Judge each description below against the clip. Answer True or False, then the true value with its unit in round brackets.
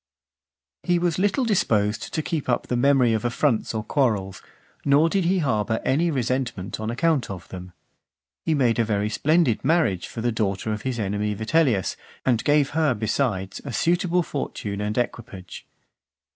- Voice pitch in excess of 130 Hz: False (120 Hz)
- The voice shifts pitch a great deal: True (6.4 semitones)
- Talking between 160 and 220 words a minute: True (170 wpm)